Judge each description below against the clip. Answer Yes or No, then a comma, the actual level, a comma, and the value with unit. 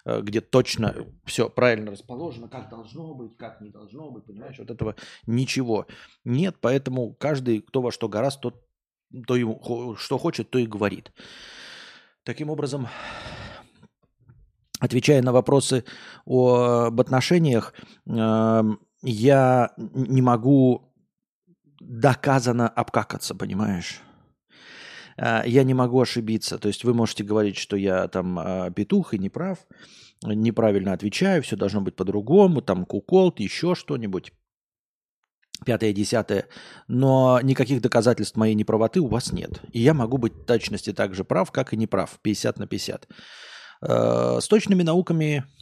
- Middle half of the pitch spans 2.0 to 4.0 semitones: Yes, average, 3.7 semitones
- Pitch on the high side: No, low, 120 Hz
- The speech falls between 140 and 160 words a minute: No, average, 130 wpm